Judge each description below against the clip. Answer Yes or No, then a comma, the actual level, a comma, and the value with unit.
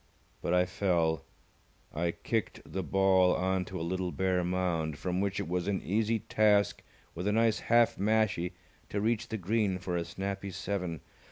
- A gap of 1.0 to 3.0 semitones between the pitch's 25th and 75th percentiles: Yes, narrow, 2.4 semitones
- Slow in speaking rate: No, average, 175 wpm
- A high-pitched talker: No, very low, 95 Hz